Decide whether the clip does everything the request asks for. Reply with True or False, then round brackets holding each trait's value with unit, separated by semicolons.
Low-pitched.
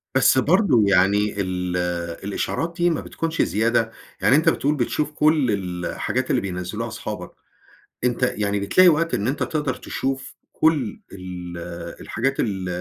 True (120 Hz)